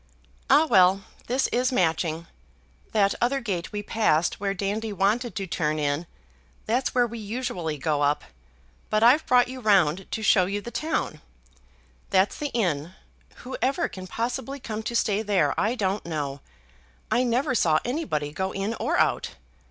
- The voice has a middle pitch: No, high, 205 Hz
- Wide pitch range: Yes, wide, 5.7 semitones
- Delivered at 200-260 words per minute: No, average, 160 wpm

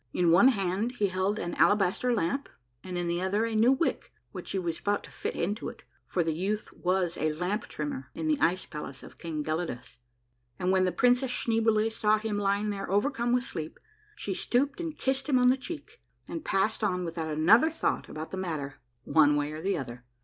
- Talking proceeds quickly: Yes, fast, 210 wpm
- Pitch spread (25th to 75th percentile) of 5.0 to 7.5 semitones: Yes, wide, 5.6 semitones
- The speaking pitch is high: Yes, high, 195 Hz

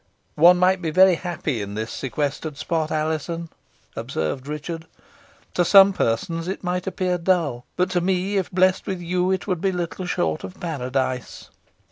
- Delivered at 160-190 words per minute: Yes, average, 165 wpm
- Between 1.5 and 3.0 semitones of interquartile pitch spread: No, average, 3.6 semitones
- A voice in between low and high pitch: Yes, medium, 170 Hz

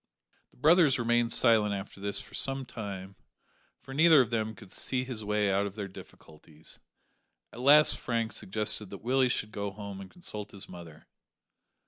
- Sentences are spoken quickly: No, average, 170 wpm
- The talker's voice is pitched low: Yes, low, 110 Hz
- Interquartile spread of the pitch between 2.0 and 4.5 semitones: Yes, average, 4.2 semitones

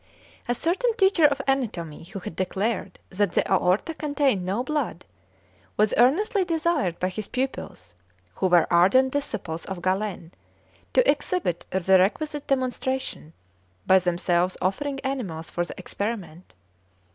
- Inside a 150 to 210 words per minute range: No, slow, 135 wpm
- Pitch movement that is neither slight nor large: No, wide, 7.7 semitones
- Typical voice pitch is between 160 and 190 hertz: No, high, 215 Hz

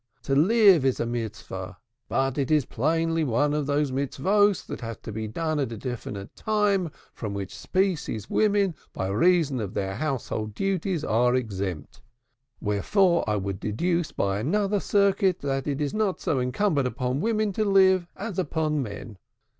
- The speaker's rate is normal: Yes, average, 165 wpm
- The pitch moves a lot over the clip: Yes, wide, 8.6 semitones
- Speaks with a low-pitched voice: No, medium, 145 Hz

